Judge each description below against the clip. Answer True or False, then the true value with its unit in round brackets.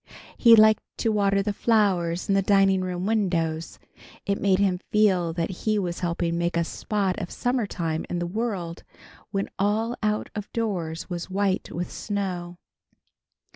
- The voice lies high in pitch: True (195 Hz)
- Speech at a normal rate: True (160 wpm)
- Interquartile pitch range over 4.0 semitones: False (3.2 semitones)